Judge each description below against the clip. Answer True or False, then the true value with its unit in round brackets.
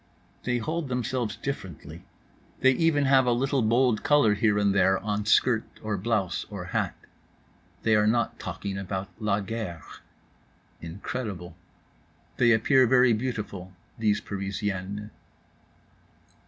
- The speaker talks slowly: True (125 wpm)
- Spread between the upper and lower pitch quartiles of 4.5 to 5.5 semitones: False (3.9 semitones)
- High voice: False (110 Hz)